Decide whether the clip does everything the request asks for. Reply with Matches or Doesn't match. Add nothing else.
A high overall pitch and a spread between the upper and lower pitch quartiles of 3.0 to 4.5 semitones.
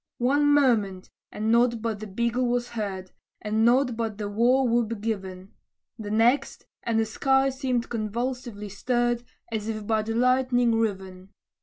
Doesn't match